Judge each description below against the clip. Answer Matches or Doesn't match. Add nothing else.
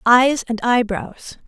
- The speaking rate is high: Doesn't match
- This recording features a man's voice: Doesn't match